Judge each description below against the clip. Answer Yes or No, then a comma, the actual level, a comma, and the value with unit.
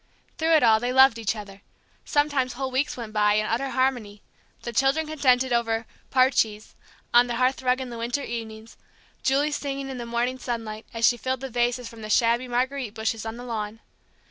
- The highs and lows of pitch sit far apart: No, narrow, 2.6 semitones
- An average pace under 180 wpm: No, average, 195 wpm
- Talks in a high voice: Yes, high, 240 Hz